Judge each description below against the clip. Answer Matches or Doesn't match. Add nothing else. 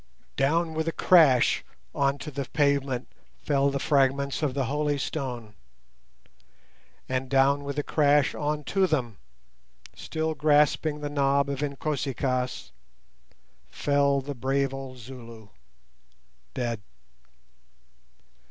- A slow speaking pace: Matches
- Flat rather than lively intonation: Matches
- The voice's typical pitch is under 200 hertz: Matches